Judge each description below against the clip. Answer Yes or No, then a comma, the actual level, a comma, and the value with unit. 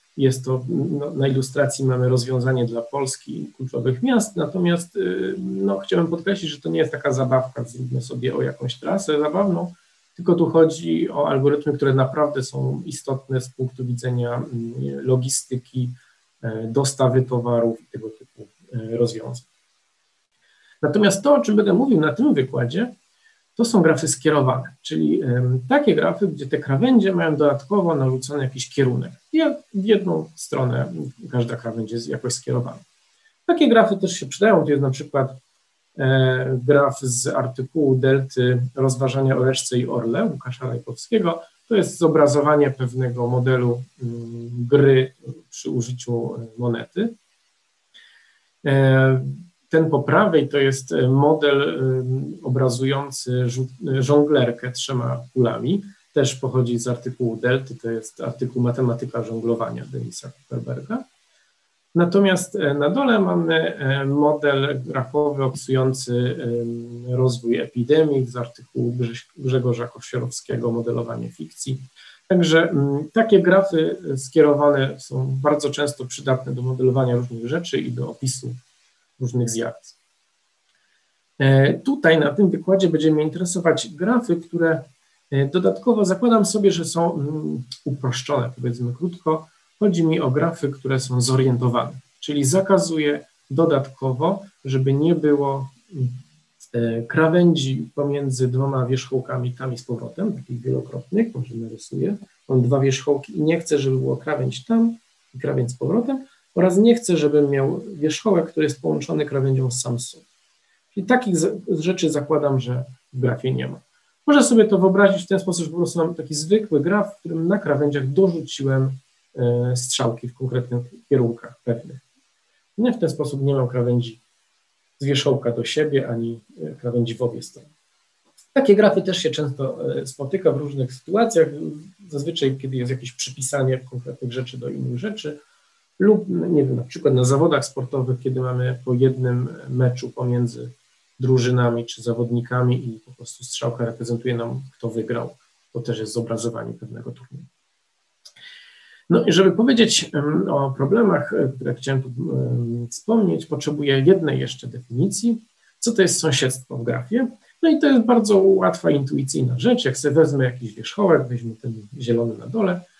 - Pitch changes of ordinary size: Yes, average, 4.5 semitones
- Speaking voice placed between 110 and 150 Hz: Yes, low, 135 Hz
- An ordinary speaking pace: Yes, average, 140 wpm